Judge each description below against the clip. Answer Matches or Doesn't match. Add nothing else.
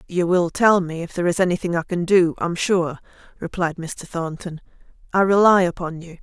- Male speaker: Doesn't match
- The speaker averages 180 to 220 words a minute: Matches